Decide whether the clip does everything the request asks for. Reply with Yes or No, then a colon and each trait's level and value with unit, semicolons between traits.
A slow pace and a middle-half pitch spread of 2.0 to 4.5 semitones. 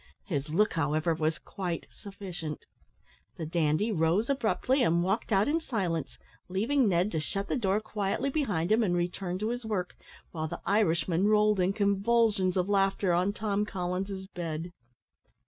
No: average, 160 wpm; average, 3.6 semitones